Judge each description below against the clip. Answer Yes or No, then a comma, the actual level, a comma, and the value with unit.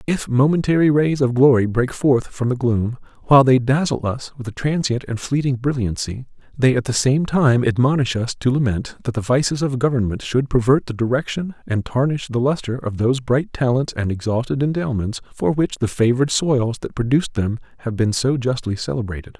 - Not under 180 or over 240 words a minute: Yes, average, 190 wpm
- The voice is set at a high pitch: No, low, 130 Hz